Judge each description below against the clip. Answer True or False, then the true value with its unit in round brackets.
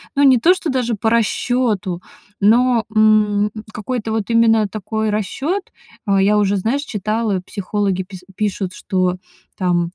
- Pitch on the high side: True (215 Hz)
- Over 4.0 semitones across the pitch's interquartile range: False (2.9 semitones)